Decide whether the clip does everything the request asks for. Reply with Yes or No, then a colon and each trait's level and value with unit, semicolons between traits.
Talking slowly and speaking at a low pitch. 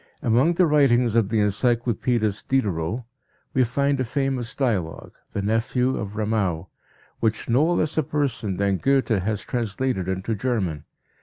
No: average, 145 wpm; low, 115 Hz